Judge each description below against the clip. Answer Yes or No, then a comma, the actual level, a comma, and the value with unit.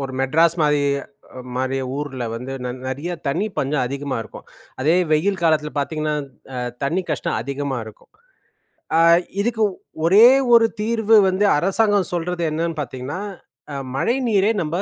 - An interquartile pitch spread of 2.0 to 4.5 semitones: No, wide, 5.4 semitones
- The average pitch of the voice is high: No, medium, 155 Hz